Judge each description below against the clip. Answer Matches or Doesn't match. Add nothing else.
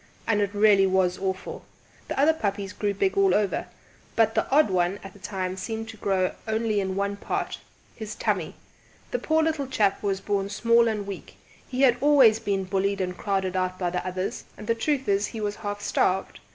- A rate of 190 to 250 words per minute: Matches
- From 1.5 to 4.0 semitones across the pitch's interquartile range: Matches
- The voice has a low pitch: Doesn't match